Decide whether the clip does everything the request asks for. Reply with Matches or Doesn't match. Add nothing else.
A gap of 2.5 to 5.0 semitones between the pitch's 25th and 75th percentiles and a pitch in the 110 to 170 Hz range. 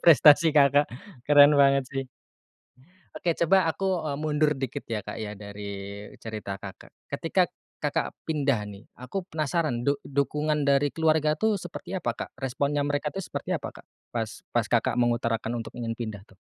Matches